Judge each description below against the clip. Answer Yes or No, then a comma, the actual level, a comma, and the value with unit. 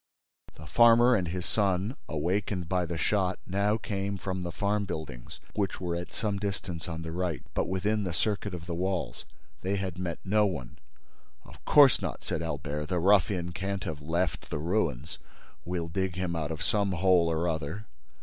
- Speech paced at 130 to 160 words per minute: No, average, 180 wpm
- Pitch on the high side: No, very low, 90 Hz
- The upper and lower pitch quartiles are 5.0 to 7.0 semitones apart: No, average, 3.3 semitones